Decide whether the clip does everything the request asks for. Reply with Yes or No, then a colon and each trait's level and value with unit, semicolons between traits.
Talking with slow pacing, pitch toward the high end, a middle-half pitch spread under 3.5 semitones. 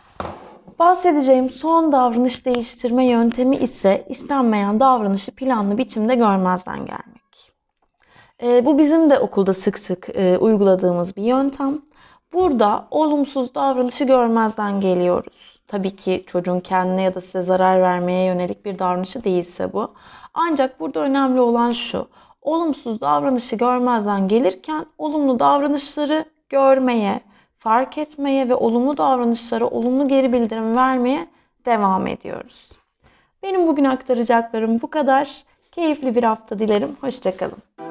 No: slow, 120 wpm; high, 245 Hz; average, 5.1 semitones